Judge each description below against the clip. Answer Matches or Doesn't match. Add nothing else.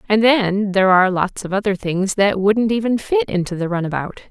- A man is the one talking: Doesn't match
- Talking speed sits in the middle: Doesn't match